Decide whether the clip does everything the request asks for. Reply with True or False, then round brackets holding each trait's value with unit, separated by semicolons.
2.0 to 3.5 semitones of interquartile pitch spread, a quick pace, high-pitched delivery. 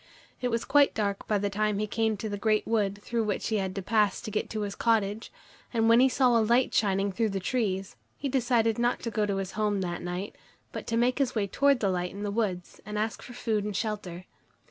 True (2.6 semitones; 250 wpm; 215 Hz)